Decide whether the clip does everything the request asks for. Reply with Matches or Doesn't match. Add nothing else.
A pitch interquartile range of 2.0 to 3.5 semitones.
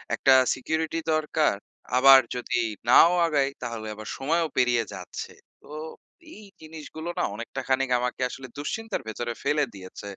Doesn't match